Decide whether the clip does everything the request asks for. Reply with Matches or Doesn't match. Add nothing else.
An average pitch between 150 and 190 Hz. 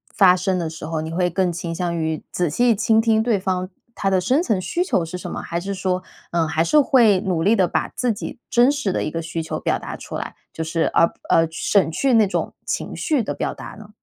Matches